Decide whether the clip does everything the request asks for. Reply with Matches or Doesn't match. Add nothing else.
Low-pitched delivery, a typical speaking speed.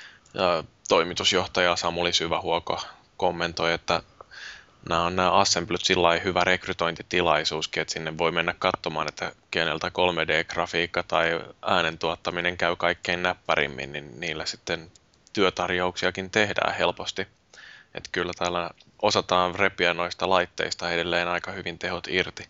Matches